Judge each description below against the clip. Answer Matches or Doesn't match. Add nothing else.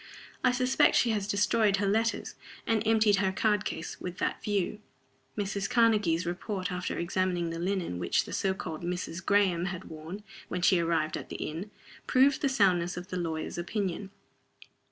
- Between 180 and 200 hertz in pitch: Matches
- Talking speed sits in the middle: Matches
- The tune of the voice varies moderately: Matches